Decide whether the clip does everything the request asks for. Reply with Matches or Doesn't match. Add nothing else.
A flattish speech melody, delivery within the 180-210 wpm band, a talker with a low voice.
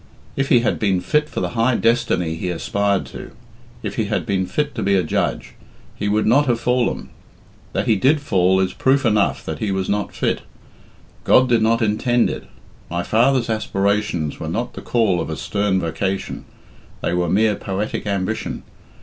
Doesn't match